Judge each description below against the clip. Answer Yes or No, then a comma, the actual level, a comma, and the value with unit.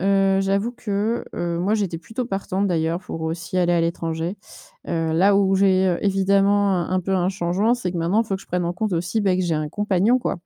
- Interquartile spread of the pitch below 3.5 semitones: Yes, average, 2.7 semitones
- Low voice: No, high, 190 Hz